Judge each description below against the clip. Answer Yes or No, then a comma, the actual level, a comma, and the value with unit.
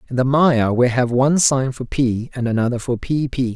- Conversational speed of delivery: No, fast, 235 wpm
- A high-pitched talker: No, low, 130 Hz